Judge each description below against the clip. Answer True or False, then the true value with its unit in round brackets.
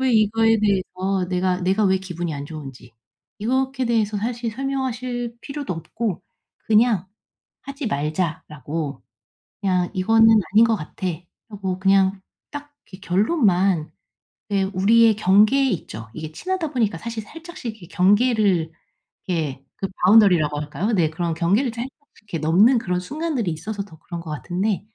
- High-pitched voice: True (195 Hz)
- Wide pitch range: False (4.7 semitones)